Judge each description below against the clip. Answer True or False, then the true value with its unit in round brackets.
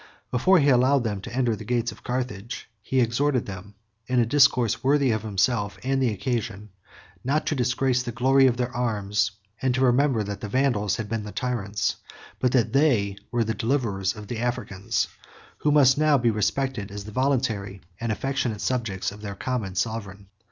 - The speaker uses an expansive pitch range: False (4.0 semitones)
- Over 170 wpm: True (185 wpm)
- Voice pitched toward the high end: False (120 Hz)